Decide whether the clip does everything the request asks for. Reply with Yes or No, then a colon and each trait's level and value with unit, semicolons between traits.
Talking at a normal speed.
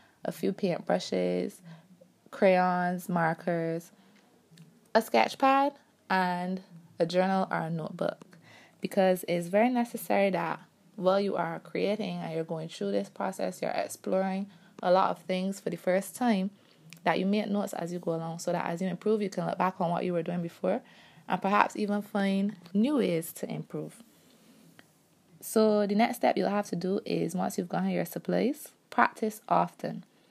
Yes: average, 170 wpm